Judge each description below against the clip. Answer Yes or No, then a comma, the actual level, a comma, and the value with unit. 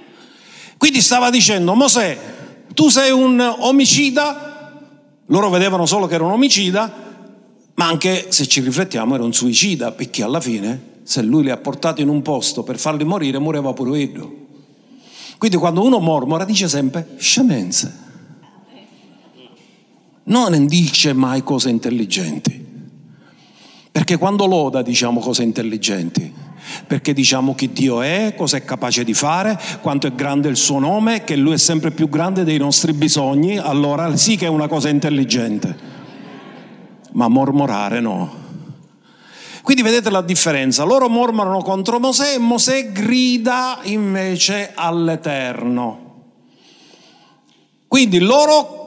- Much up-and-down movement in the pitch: Yes, wide, 8.0 semitones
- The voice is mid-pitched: Yes, medium, 170 Hz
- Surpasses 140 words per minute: No, average, 135 wpm